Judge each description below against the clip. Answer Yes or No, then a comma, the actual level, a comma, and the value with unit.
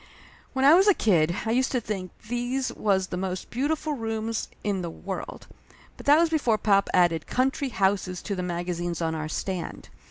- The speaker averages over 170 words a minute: Yes, average, 190 wpm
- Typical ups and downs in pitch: No, wide, 5.9 semitones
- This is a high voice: Yes, high, 205 Hz